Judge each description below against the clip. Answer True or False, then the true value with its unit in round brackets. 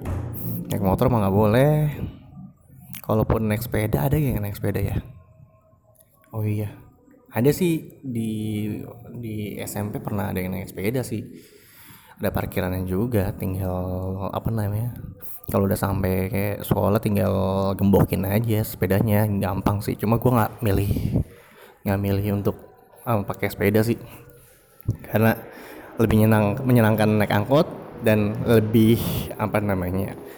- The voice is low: True (105 Hz)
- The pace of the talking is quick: False (125 wpm)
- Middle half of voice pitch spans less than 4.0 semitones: True (2.9 semitones)